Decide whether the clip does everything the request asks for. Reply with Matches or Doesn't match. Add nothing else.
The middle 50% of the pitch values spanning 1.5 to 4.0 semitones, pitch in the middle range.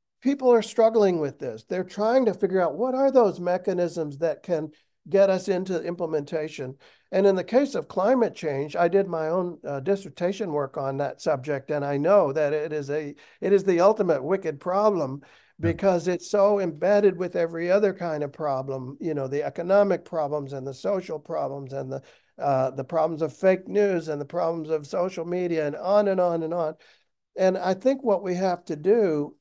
Doesn't match